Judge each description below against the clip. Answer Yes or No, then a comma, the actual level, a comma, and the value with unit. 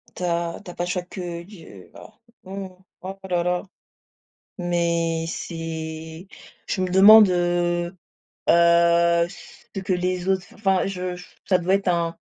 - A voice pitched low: No, medium, 175 Hz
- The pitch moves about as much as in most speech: No, narrow, 1.5 semitones